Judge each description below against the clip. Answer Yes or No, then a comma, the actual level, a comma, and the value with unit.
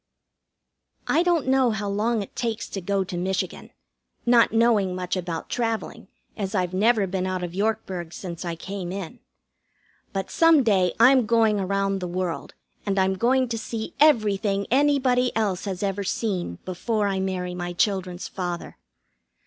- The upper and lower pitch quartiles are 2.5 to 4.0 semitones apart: Yes, average, 3.7 semitones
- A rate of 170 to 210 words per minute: No, average, 160 wpm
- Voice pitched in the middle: No, high, 200 Hz